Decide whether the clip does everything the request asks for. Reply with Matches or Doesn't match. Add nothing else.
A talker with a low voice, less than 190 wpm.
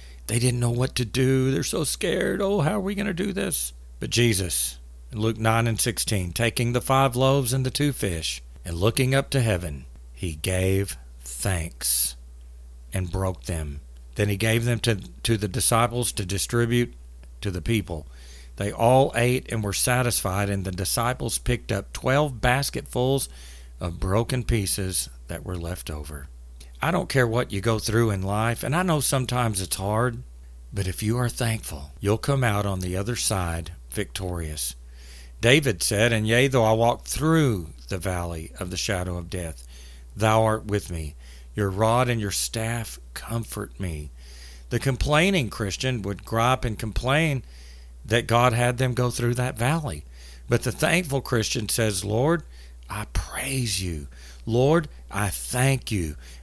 Matches